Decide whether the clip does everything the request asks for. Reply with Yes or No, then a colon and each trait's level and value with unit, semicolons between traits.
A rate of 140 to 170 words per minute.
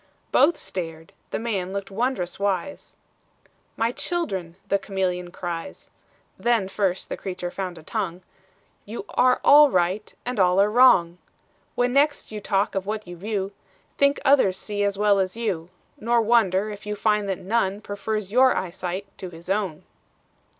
Yes: average, 160 wpm